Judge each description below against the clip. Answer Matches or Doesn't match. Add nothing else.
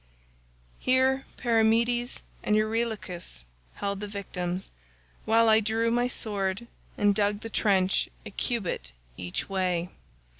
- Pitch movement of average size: Matches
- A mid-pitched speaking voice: Doesn't match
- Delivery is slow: Matches